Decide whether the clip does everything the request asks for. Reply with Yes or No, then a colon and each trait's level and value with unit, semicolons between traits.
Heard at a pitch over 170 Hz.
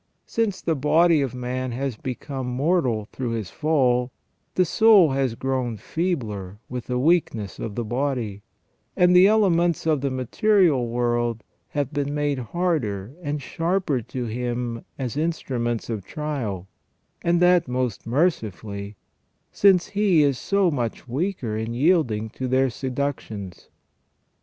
No: low, 130 Hz